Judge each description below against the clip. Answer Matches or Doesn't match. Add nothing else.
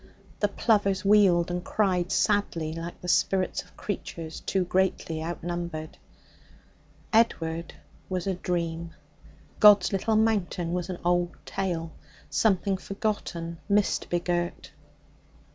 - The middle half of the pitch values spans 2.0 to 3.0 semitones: Matches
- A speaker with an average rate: Doesn't match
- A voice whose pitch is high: Doesn't match